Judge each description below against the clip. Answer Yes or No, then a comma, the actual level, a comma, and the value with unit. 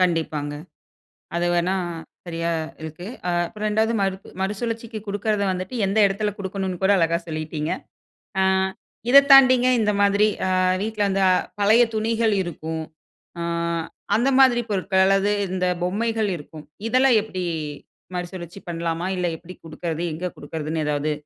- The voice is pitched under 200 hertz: Yes, high, 190 Hz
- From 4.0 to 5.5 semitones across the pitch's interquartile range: Yes, average, 4.3 semitones